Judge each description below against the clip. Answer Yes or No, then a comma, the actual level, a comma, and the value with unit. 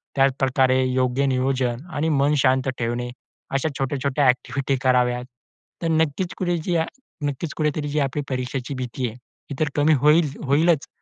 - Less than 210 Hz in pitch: Yes, low, 135 Hz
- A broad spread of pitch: No, narrow, 2.6 semitones